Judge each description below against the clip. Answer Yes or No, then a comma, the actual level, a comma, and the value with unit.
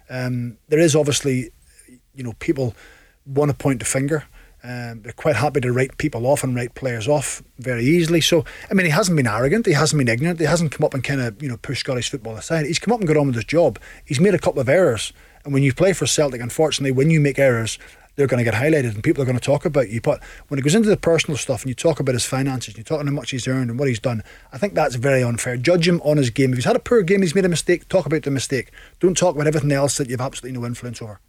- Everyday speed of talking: No, fast, 285 wpm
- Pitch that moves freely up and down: No, average, 3.8 semitones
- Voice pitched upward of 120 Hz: Yes, medium, 140 Hz